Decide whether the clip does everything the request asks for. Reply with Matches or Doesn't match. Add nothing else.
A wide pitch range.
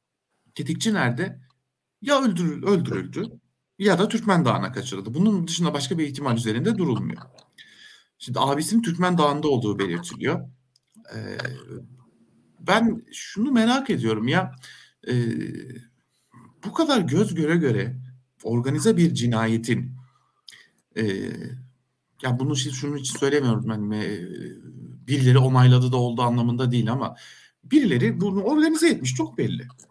Matches